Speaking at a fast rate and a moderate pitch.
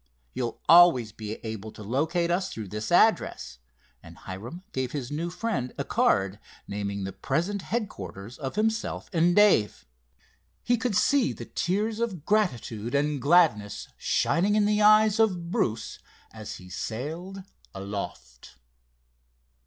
No: slow, 135 wpm; medium, 150 Hz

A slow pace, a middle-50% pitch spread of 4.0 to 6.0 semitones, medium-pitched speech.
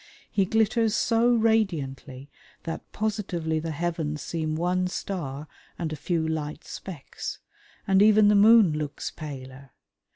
Yes: slow, 130 wpm; wide, 5.4 semitones; medium, 170 Hz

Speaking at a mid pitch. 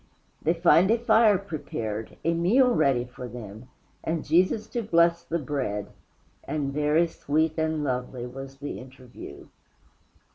Yes: medium, 155 Hz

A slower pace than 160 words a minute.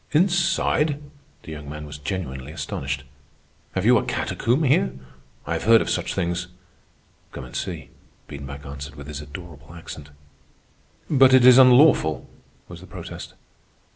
Yes: average, 145 wpm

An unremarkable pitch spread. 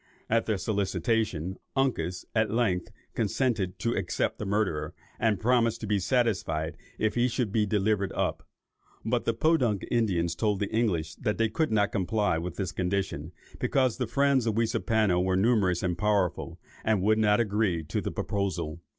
Yes: average, 3.7 semitones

